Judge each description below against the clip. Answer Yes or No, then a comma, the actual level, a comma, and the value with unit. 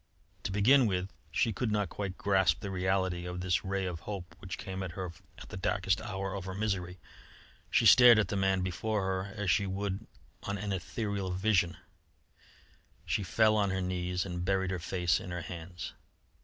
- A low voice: Yes, very low, 95 Hz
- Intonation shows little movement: Yes, narrow, 2.0 semitones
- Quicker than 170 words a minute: Yes, average, 190 wpm